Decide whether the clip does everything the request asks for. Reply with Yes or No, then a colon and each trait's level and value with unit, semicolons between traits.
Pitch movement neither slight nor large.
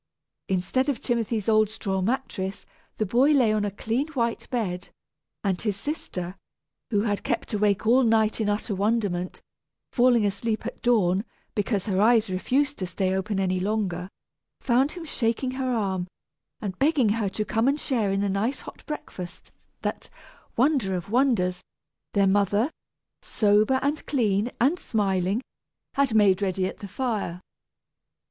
Yes: average, 4.1 semitones